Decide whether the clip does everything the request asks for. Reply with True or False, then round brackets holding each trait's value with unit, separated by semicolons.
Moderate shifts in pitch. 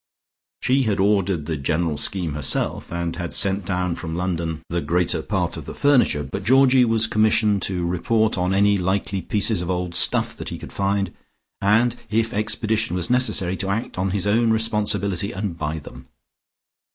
True (3.9 semitones)